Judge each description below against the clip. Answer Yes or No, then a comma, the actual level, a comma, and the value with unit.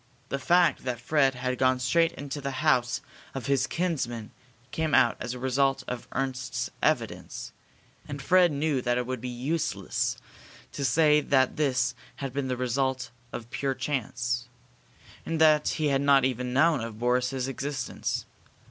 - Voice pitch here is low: Yes, low, 130 Hz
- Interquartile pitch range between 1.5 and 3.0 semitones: Yes, narrow, 2.4 semitones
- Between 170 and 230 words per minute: No, average, 160 wpm